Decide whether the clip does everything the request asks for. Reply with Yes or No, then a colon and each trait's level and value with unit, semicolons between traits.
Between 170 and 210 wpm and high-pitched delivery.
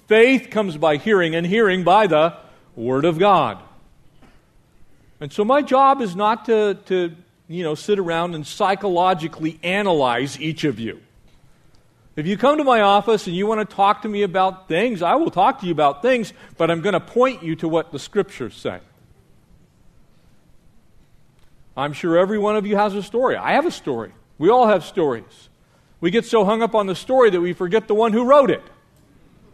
Yes: average, 195 wpm; high, 195 Hz